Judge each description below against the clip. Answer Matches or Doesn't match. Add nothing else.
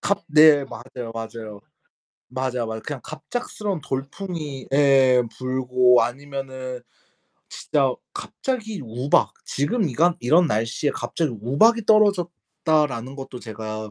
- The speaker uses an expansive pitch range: Doesn't match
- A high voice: Doesn't match